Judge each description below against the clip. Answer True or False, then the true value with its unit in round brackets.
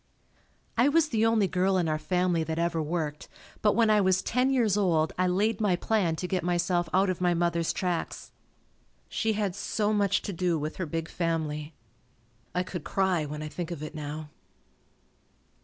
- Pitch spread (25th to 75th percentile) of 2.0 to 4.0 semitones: True (3.6 semitones)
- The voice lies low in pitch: False (180 Hz)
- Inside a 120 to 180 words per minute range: False (190 wpm)